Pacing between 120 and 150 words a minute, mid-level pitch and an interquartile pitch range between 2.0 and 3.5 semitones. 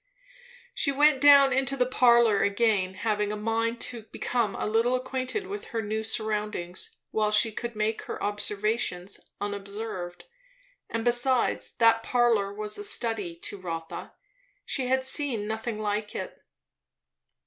No: average, 140 wpm; high, 225 Hz; average, 3.0 semitones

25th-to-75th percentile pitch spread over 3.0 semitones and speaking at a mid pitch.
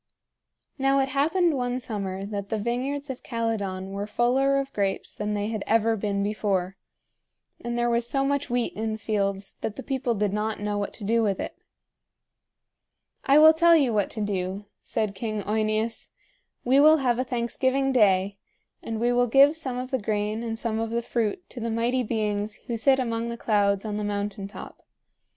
No: average, 3.6 semitones; high, 225 Hz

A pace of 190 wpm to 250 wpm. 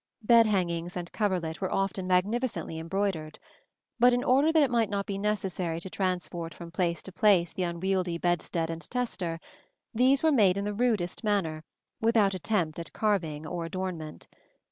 No: average, 165 wpm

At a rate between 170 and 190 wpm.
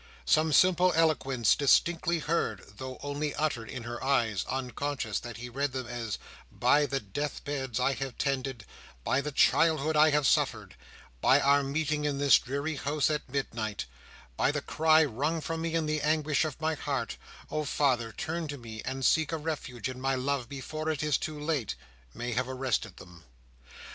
Yes: average, 180 wpm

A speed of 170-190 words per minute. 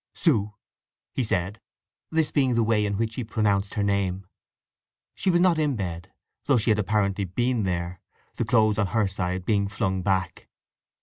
Yes: average, 175 wpm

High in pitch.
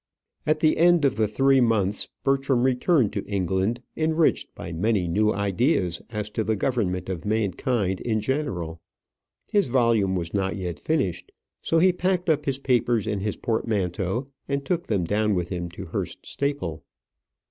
No: low, 110 Hz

